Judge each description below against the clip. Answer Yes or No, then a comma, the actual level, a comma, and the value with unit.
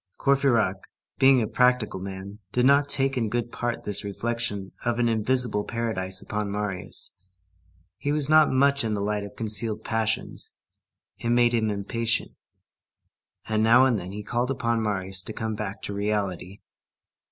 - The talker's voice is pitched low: Yes, low, 110 Hz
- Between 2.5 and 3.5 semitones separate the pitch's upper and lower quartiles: Yes, average, 3.0 semitones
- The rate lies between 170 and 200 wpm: No, average, 160 wpm